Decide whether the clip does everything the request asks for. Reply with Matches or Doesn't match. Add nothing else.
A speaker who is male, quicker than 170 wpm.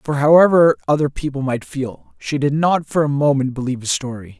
Matches